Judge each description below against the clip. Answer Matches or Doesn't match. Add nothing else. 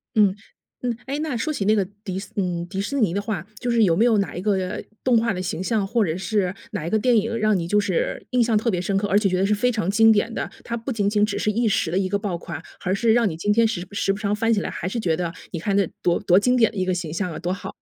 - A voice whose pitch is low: Doesn't match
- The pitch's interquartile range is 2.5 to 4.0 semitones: Matches